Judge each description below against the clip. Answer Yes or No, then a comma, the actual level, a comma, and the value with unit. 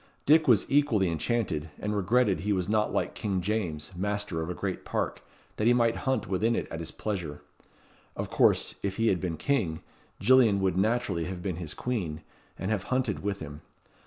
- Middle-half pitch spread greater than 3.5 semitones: Yes, average, 4.5 semitones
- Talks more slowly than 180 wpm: No, average, 190 wpm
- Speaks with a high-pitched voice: No, low, 100 Hz